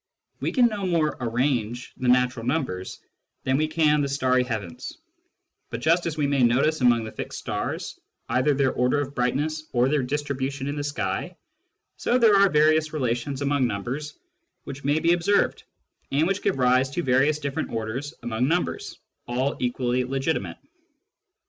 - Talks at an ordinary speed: Yes, average, 170 wpm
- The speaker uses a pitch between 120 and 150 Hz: Yes, medium, 140 Hz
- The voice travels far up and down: No, average, 3.5 semitones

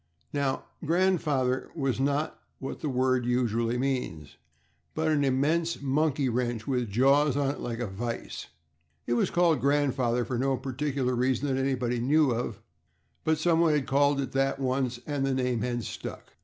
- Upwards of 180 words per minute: No, average, 165 wpm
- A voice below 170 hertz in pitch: Yes, low, 135 Hz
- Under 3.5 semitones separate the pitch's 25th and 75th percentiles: Yes, average, 2.7 semitones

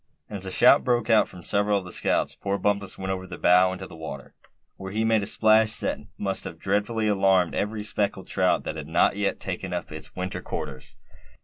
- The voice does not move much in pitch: Yes, narrow, 2.3 semitones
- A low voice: Yes, very low, 95 Hz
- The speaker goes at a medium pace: No, fast, 220 wpm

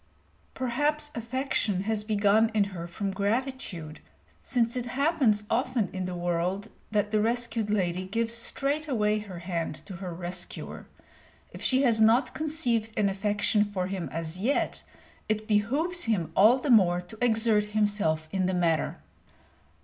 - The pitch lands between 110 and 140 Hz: No, high, 210 Hz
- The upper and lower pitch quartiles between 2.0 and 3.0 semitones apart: No, average, 4.2 semitones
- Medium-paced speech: Yes, average, 150 wpm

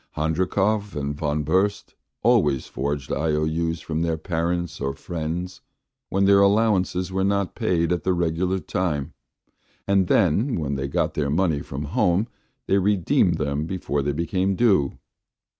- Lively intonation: No, average, 4.1 semitones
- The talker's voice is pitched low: Yes, very low, 85 Hz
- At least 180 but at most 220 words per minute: No, average, 145 wpm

